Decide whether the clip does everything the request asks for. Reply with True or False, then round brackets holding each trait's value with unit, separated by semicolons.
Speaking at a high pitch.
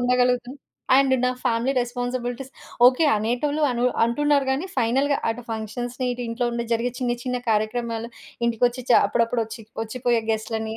True (245 Hz)